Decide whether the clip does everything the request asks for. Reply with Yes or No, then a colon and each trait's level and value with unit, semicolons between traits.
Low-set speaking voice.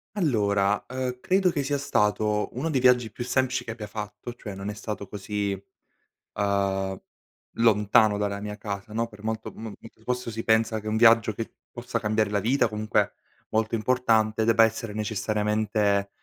Yes: low, 110 Hz